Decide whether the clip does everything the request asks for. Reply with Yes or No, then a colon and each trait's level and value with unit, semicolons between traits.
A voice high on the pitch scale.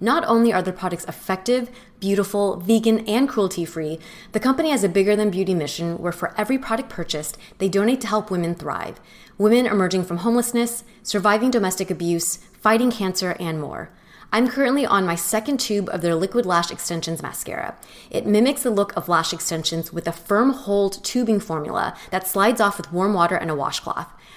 Yes: high, 200 Hz